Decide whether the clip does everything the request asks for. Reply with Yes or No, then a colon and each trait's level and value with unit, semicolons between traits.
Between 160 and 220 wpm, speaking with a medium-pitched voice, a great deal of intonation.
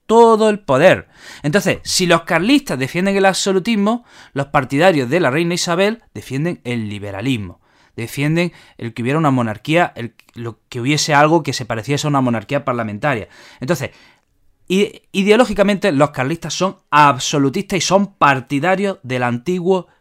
No: average, 140 wpm; medium, 150 Hz; wide, 6.6 semitones